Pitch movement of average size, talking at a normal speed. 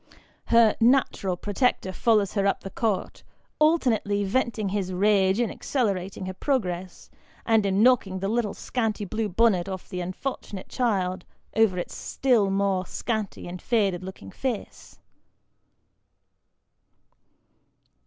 No: average, 3.5 semitones; slow, 130 wpm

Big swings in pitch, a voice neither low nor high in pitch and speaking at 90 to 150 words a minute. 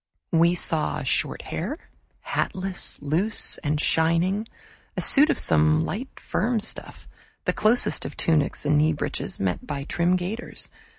Yes: wide, 5.9 semitones; medium, 170 Hz; slow, 135 wpm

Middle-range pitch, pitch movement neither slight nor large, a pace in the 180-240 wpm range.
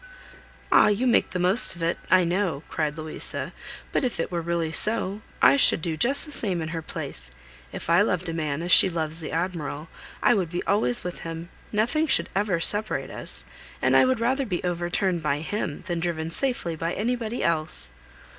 Yes: medium, 175 Hz; average, 4.4 semitones; average, 200 wpm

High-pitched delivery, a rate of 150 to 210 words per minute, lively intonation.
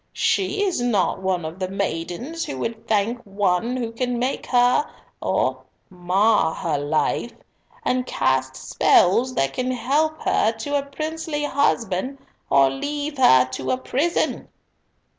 No: high, 230 Hz; average, 140 wpm; wide, 7.6 semitones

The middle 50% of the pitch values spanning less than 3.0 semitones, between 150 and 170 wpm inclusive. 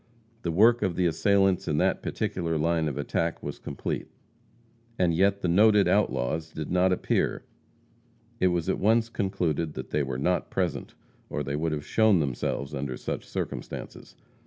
No: average, 4.1 semitones; average, 165 wpm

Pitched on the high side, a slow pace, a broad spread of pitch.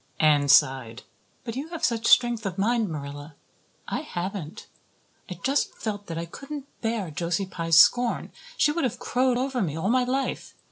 No: high, 205 Hz; average, 175 wpm; wide, 7.3 semitones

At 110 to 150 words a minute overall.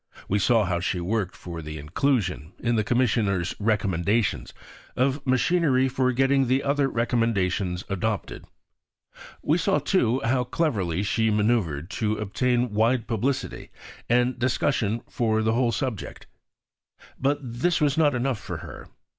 Yes: average, 140 wpm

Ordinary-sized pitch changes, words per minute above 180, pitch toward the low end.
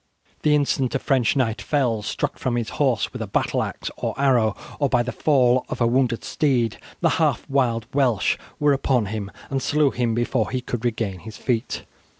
Yes: average, 3.0 semitones; average, 195 wpm; low, 125 Hz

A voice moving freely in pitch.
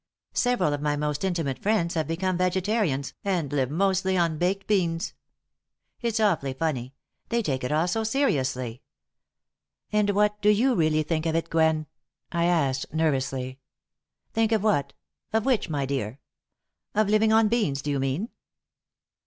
Yes: wide, 6.5 semitones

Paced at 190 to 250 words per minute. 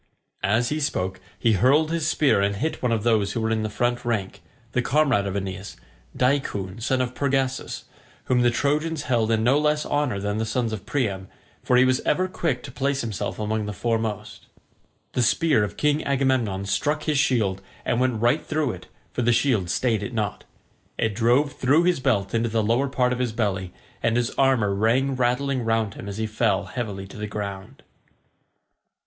Yes: average, 195 wpm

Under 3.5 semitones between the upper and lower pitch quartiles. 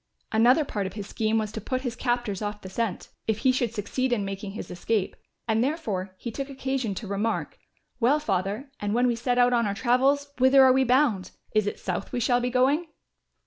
No: average, 3.8 semitones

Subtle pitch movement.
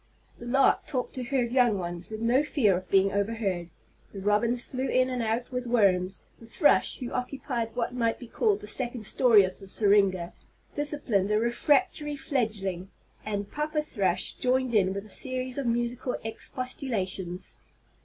No: average, 4.4 semitones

